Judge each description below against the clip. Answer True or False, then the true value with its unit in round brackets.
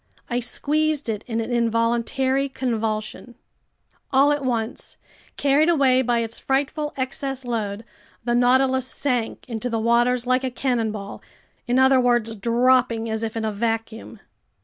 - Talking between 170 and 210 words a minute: False (145 wpm)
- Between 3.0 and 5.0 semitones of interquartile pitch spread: False (2.5 semitones)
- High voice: True (245 Hz)